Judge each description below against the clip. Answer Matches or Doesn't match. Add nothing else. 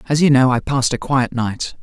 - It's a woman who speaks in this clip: Doesn't match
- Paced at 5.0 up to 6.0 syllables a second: Matches